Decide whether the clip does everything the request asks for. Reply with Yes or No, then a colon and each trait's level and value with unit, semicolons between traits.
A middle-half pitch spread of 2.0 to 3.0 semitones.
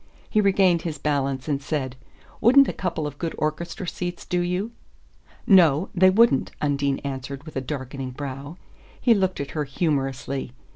No: average, 4.7 semitones